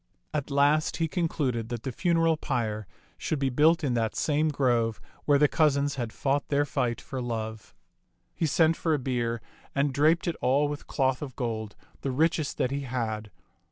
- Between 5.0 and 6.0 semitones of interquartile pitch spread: No, average, 3.9 semitones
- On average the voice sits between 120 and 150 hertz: Yes, medium, 140 Hz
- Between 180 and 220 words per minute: Yes, average, 185 wpm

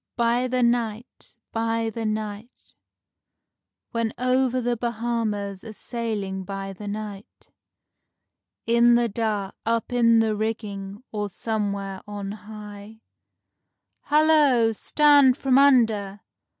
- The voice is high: Yes, high, 225 Hz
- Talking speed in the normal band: No, slow, 110 wpm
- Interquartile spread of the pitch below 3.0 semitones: Yes, narrow, 2.6 semitones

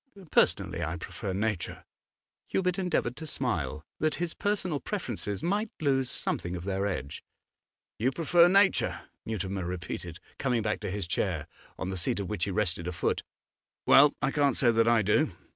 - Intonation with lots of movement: Yes, wide, 8.7 semitones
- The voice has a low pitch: Yes, low, 110 Hz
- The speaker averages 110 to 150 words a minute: No, average, 170 wpm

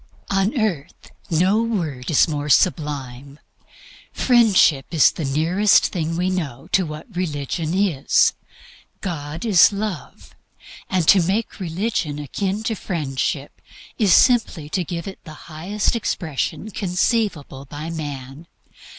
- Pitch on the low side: No, medium, 170 Hz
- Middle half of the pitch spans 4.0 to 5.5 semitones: Yes, average, 5.1 semitones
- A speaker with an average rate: No, slow, 125 wpm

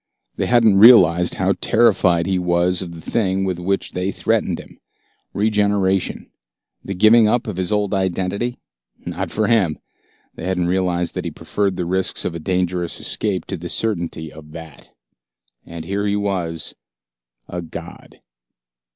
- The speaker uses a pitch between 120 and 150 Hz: No, very low, 95 Hz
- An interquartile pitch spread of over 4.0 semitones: No, average, 2.8 semitones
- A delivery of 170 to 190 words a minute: No, average, 155 wpm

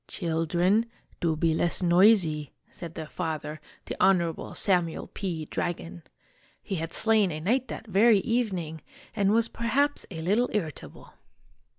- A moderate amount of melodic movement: Yes, average, 4.9 semitones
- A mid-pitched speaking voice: Yes, medium, 180 Hz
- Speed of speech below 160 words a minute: Yes, average, 150 wpm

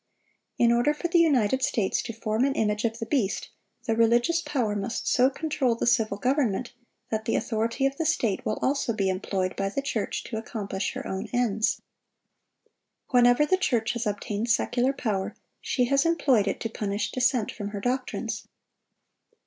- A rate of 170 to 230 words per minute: Yes, average, 175 wpm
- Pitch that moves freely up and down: No, average, 3.8 semitones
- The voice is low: No, high, 230 Hz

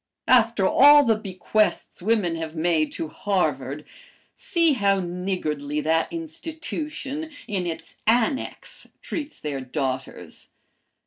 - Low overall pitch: No, high, 195 Hz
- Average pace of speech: No, slow, 110 wpm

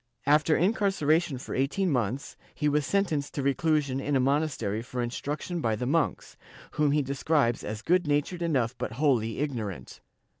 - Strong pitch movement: No, average, 3.8 semitones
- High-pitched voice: No, medium, 145 Hz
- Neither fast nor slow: Yes, average, 160 wpm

